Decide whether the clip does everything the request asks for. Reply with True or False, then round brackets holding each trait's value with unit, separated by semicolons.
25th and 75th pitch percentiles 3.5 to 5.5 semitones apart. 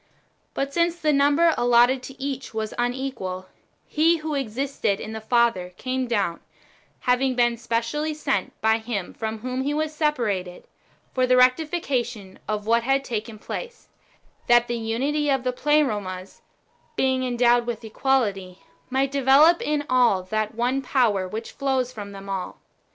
True (3.8 semitones)